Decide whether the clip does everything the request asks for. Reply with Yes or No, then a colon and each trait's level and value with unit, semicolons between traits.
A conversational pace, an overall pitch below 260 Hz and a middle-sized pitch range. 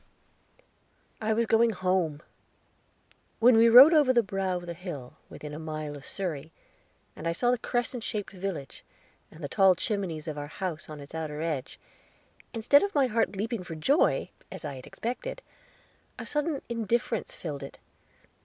No: average, 170 wpm; high, 190 Hz; wide, 7.0 semitones